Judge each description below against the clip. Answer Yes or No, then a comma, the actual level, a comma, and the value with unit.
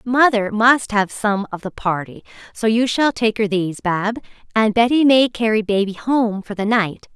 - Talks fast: No, average, 195 wpm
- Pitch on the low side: No, high, 220 Hz